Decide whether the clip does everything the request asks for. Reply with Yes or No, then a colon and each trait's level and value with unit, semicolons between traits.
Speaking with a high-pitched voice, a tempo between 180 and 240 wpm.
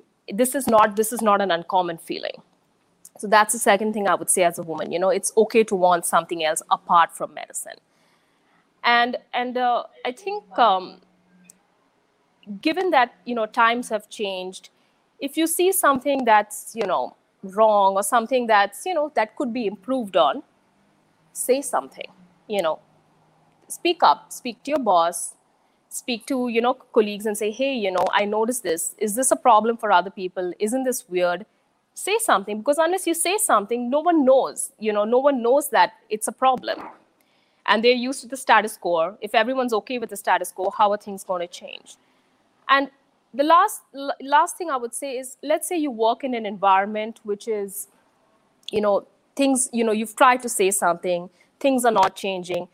Yes: high, 225 Hz; average, 190 wpm